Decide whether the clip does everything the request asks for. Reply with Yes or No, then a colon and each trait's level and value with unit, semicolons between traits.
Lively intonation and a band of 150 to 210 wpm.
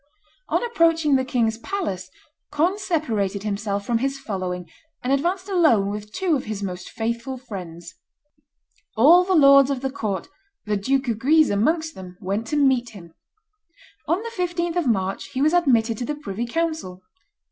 Yes: wide, 7.7 semitones; average, 170 wpm